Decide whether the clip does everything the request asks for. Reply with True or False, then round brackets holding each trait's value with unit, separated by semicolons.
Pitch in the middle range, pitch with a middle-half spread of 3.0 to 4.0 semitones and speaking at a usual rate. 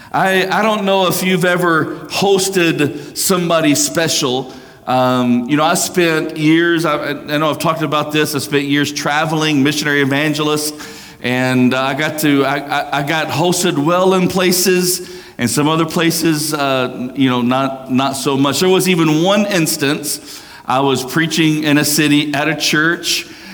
True (155 Hz; 3.4 semitones; 170 wpm)